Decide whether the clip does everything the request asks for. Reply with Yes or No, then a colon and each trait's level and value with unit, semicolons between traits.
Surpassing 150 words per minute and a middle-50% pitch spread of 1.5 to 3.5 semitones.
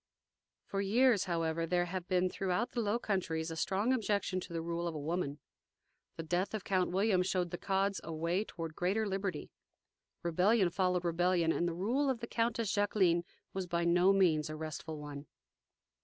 Yes: average, 185 wpm; average, 3.0 semitones